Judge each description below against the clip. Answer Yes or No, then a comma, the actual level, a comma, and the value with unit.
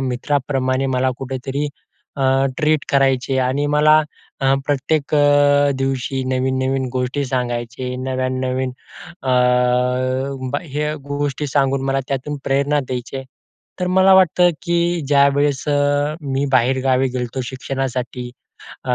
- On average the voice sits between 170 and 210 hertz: No, low, 135 Hz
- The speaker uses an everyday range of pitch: No, narrow, 1.8 semitones